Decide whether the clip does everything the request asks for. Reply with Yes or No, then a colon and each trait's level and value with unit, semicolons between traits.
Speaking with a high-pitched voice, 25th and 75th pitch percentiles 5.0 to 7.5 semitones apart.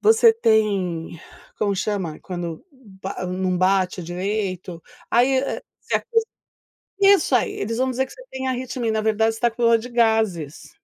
Yes: high, 220 Hz; average, 5.3 semitones